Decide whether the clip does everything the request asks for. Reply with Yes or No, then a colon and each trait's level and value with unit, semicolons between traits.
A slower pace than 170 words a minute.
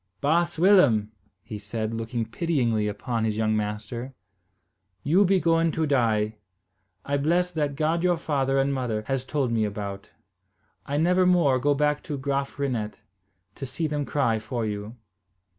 Yes: average, 160 wpm